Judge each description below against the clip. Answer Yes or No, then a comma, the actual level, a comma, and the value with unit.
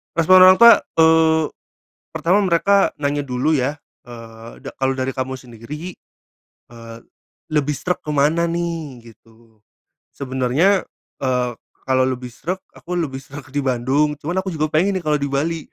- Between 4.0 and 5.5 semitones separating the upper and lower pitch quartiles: Yes, average, 4.4 semitones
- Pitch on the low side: No, medium, 145 Hz